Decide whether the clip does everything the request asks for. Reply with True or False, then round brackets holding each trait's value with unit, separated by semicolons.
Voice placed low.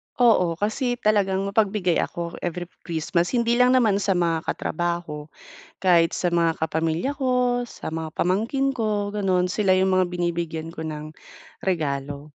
False (180 Hz)